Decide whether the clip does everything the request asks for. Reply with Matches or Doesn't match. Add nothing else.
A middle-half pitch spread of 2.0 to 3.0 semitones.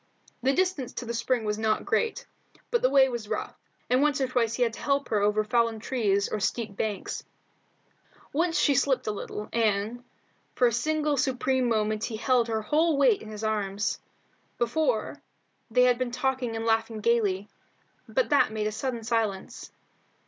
Doesn't match